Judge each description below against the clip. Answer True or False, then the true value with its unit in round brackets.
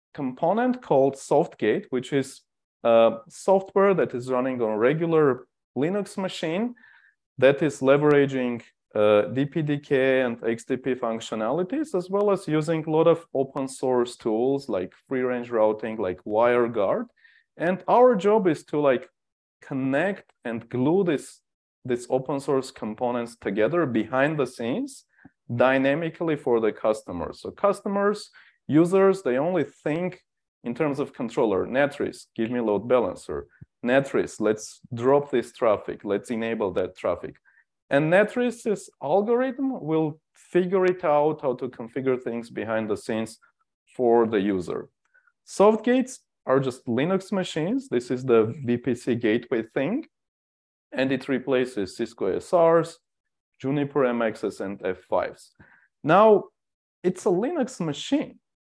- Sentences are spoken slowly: True (130 wpm)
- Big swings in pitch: True (7.4 semitones)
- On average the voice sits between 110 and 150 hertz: True (140 Hz)